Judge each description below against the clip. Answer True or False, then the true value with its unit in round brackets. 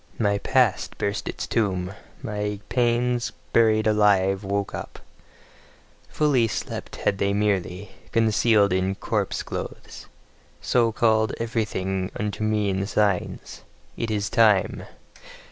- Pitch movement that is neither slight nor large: False (2.3 semitones)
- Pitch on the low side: True (105 Hz)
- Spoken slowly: True (115 wpm)